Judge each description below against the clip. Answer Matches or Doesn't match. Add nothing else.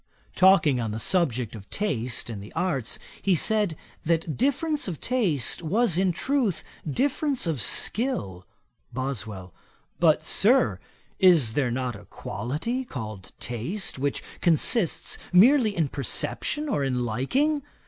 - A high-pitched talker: Doesn't match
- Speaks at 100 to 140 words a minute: Matches